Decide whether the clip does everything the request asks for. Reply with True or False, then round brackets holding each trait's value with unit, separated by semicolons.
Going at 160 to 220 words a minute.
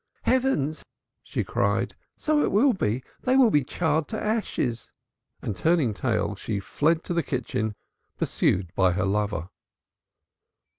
False (140 wpm)